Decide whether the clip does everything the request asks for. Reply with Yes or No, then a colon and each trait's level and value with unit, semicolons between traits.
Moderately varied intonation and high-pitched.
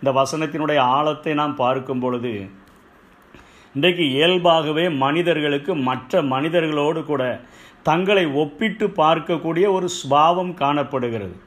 No: average, 4.2 semitones; medium, 155 Hz